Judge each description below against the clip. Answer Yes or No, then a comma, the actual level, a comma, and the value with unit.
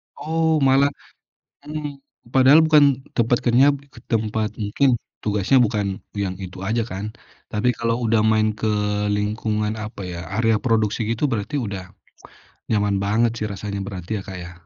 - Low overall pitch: Yes, low, 110 Hz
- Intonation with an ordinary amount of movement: Yes, average, 3.8 semitones